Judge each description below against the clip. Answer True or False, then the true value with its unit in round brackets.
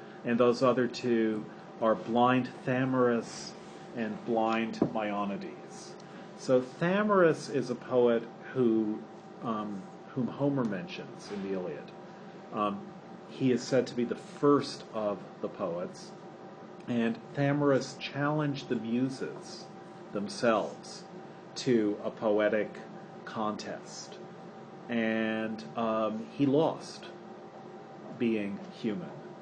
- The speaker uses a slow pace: True (100 wpm)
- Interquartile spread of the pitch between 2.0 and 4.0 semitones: False (4.5 semitones)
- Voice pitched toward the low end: True (125 Hz)